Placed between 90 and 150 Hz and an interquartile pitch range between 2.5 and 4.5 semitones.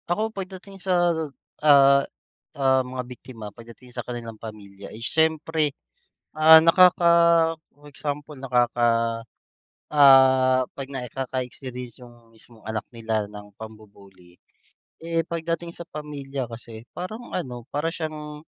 No: low, 135 Hz; wide, 5.5 semitones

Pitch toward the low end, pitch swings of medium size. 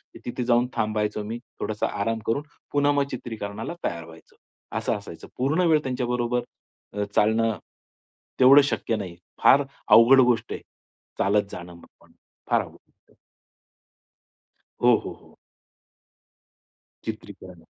Yes: low, 115 Hz; average, 3.6 semitones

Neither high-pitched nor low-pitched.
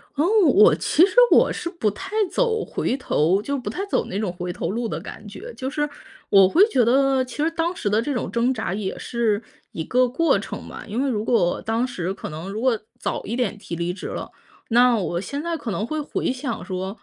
No: high, 235 Hz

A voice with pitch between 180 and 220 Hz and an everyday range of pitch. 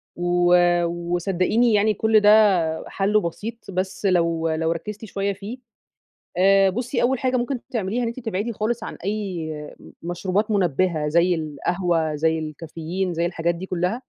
Yes: medium, 185 Hz; average, 3.9 semitones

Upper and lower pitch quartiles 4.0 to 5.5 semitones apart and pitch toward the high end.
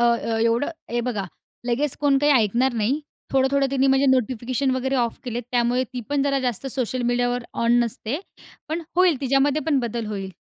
No: narrow, 2.5 semitones; very high, 255 Hz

